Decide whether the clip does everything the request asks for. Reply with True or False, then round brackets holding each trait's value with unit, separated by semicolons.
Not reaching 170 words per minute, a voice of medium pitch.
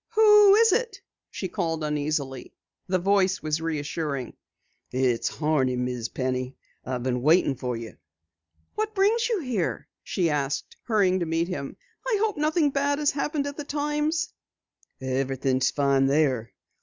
True (145 wpm; 165 Hz)